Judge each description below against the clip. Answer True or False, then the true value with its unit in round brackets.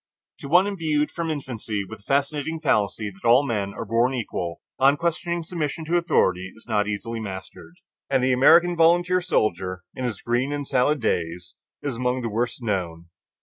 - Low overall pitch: True (125 Hz)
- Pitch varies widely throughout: True (6.8 semitones)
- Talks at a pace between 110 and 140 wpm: False (175 wpm)